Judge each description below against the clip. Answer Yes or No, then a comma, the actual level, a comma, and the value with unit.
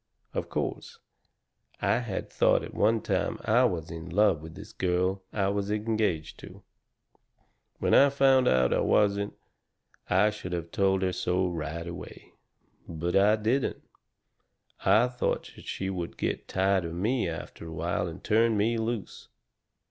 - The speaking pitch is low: Yes, very low, 95 Hz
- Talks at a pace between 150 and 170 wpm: Yes, average, 155 wpm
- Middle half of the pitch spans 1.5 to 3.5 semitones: No, average, 4.2 semitones